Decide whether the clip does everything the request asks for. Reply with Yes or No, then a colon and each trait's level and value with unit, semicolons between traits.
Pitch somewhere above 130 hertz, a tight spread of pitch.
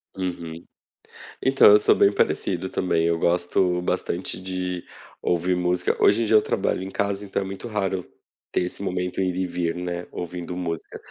No: very low, 90 Hz; narrow, 1.6 semitones